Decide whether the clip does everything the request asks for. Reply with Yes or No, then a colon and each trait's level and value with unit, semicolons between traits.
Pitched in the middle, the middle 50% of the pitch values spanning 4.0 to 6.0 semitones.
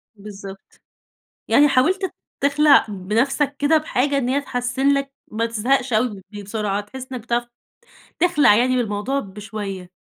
No: high, 245 Hz; average, 5.0 semitones